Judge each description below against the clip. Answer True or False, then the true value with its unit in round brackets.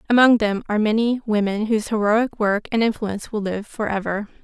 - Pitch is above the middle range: True (215 Hz)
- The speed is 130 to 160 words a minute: False (175 wpm)